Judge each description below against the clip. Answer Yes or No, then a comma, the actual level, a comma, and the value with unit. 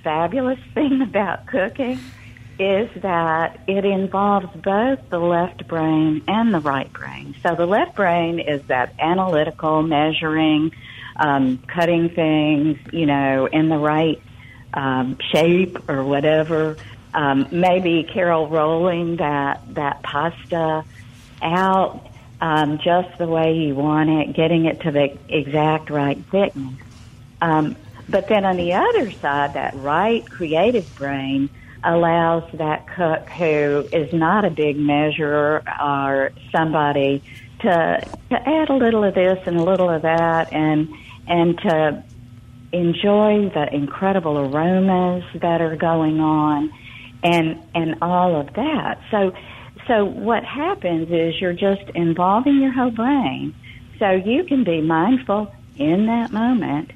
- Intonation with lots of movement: No, average, 4.3 semitones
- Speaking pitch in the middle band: Yes, medium, 160 Hz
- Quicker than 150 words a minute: No, slow, 135 wpm